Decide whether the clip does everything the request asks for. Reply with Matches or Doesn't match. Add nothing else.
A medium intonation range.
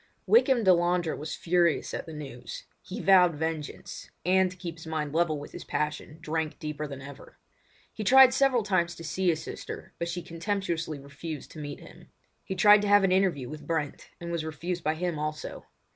Matches